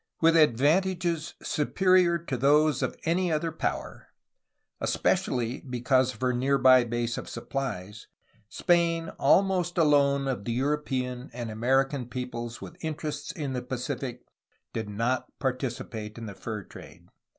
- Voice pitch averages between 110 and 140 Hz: Yes, low, 135 Hz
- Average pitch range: Yes, average, 4.4 semitones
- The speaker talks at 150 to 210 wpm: No, average, 140 wpm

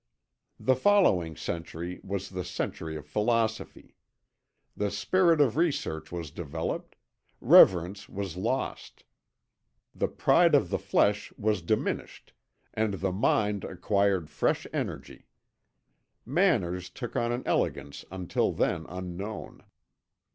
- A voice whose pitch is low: Yes, low, 100 Hz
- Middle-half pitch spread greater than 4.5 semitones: No, average, 4.2 semitones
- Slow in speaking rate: Yes, slow, 110 wpm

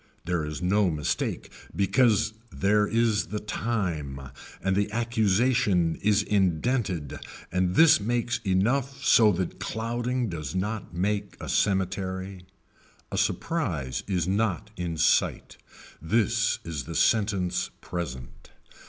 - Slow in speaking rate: Yes, slow, 120 wpm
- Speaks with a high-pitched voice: No, low, 100 Hz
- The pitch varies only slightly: No, average, 4.2 semitones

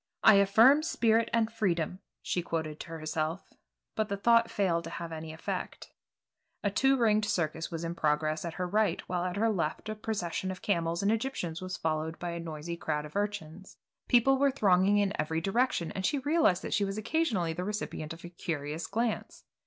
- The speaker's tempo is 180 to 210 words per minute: Yes, average, 195 wpm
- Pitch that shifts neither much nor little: Yes, average, 4.8 semitones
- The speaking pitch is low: No, medium, 185 Hz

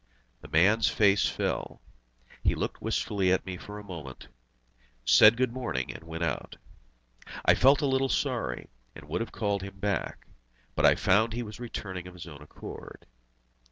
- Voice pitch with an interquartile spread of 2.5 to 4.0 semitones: No, average, 4.8 semitones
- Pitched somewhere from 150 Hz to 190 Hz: No, low, 100 Hz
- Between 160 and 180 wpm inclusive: Yes, average, 170 wpm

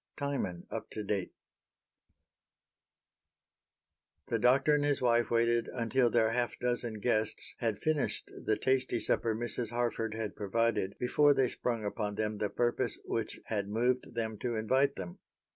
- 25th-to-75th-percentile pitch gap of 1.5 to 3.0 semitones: Yes, narrow, 2.5 semitones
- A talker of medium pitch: No, low, 115 Hz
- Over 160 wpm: No, average, 145 wpm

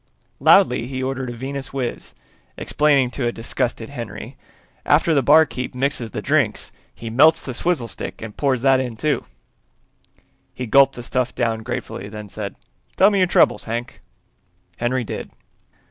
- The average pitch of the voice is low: Yes, low, 130 Hz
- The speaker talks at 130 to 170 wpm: Yes, average, 155 wpm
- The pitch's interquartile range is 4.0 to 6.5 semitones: No, average, 2.9 semitones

